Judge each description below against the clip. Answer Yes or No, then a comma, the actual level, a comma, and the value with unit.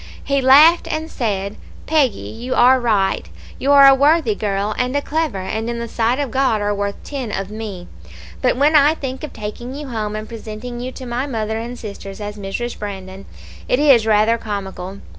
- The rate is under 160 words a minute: No, average, 200 wpm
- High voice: Yes, high, 230 Hz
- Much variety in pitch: No, average, 4.3 semitones